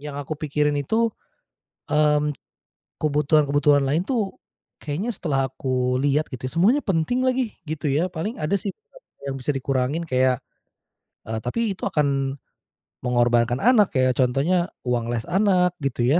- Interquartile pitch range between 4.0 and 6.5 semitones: Yes, average, 5.2 semitones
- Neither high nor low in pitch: Yes, medium, 150 Hz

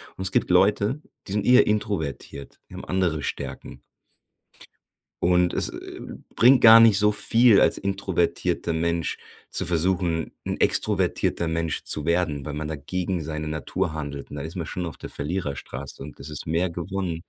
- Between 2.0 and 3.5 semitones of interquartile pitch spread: No, average, 3.9 semitones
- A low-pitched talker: Yes, very low, 85 Hz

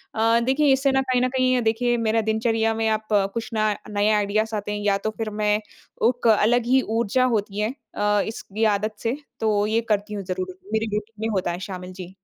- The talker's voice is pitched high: Yes, high, 220 Hz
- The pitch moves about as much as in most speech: No, narrow, 2.1 semitones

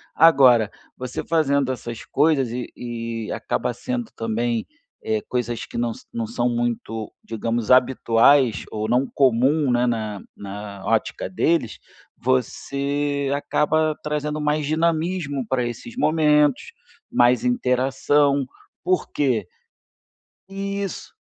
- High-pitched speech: No, low, 130 Hz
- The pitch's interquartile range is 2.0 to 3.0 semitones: No, average, 4.2 semitones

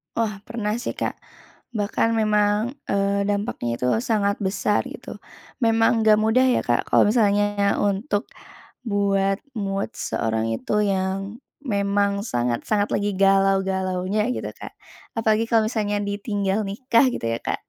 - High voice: Yes, high, 205 Hz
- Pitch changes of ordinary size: No, narrow, 1.9 semitones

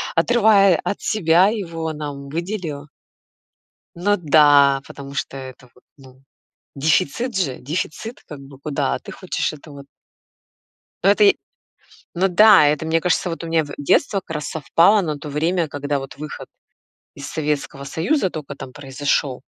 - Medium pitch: Yes, medium, 155 Hz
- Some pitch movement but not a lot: Yes, average, 4.1 semitones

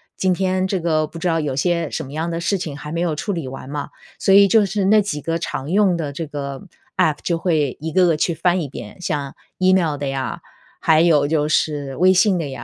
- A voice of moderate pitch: Yes, medium, 165 Hz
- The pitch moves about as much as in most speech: Yes, average, 3.8 semitones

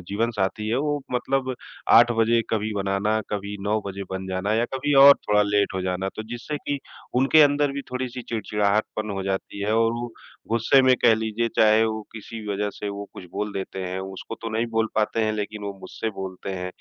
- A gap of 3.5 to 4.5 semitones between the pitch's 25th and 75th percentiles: No, average, 2.7 semitones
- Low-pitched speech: Yes, low, 110 Hz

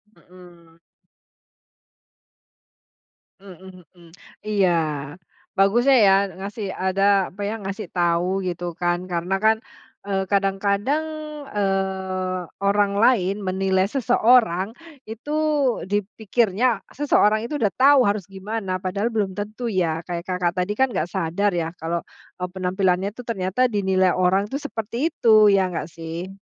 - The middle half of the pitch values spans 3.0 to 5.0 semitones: No, narrow, 2.5 semitones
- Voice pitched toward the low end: No, high, 195 Hz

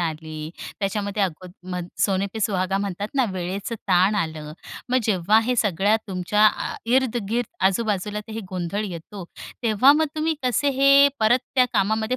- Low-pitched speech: No, high, 205 Hz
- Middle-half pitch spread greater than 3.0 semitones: Yes, average, 3.7 semitones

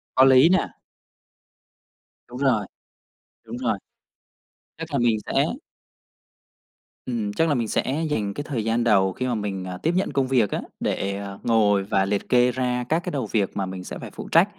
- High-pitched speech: No, low, 115 Hz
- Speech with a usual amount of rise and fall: Yes, average, 4.4 semitones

